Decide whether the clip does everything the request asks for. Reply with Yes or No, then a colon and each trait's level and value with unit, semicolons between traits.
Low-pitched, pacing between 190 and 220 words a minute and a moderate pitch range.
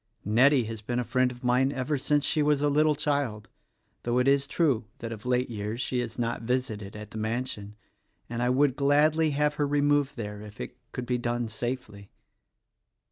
Yes: low, 125 Hz; average, 195 wpm; average, 4.0 semitones